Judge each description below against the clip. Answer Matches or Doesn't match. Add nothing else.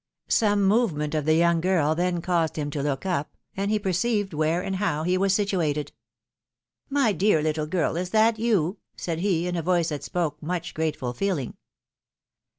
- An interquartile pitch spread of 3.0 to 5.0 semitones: Matches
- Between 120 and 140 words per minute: Doesn't match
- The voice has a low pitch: Doesn't match